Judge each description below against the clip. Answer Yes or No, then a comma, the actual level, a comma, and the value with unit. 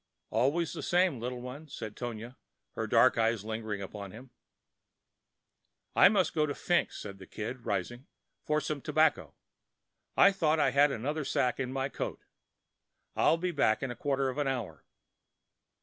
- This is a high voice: No, low, 130 Hz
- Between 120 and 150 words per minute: No, average, 165 wpm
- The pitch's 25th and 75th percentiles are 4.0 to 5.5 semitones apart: Yes, average, 4.9 semitones